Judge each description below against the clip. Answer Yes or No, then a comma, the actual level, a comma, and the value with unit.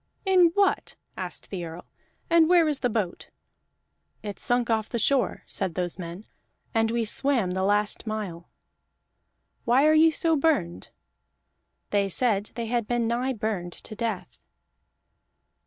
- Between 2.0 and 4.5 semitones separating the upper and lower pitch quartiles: No, average, 5.3 semitones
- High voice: Yes, high, 225 Hz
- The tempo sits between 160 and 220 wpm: No, average, 145 wpm